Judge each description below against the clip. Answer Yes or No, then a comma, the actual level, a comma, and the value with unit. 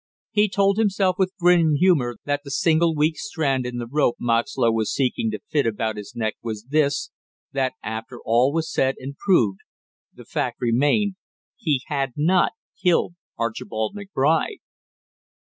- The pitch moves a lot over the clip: Yes, wide, 6.8 semitones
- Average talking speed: Yes, average, 155 wpm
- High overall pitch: No, medium, 145 Hz